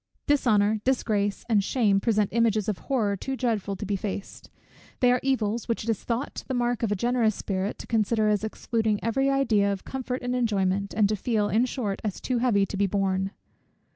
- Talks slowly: No, average, 200 wpm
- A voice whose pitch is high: Yes, high, 220 Hz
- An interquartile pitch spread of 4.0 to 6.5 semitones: No, average, 3.3 semitones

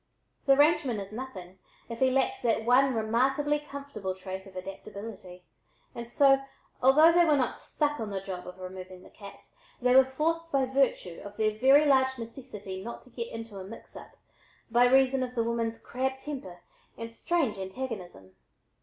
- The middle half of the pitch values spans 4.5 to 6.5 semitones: Yes, average, 5.2 semitones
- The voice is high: Yes, high, 235 Hz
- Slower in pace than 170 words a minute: No, average, 175 wpm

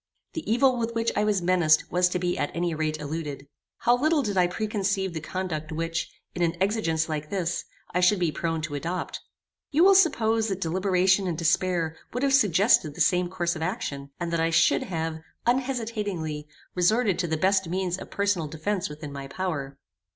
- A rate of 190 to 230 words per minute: Yes, average, 195 wpm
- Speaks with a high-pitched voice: No, medium, 180 Hz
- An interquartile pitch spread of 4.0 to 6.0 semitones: Yes, average, 4.3 semitones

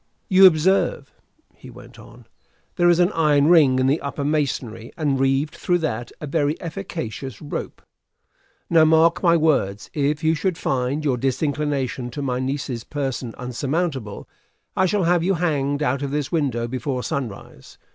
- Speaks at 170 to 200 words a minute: No, average, 160 wpm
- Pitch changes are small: No, average, 3.9 semitones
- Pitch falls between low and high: Yes, medium, 145 Hz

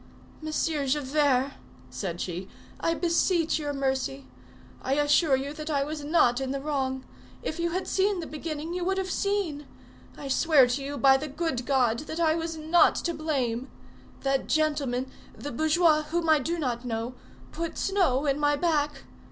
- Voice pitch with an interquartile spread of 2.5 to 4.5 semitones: Yes, average, 3.5 semitones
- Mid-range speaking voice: No, very high, 295 Hz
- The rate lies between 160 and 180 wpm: Yes, average, 175 wpm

